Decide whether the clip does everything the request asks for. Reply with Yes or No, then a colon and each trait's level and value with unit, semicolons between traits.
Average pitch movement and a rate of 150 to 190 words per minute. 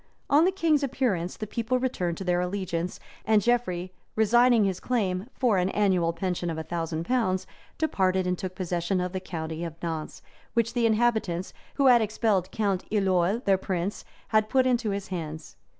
Yes: average, 4.6 semitones; average, 180 wpm